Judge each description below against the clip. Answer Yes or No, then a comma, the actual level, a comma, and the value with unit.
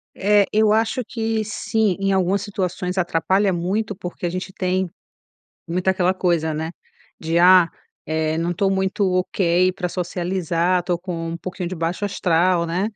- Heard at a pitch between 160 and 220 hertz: Yes, medium, 185 Hz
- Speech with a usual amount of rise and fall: No, narrow, 2.1 semitones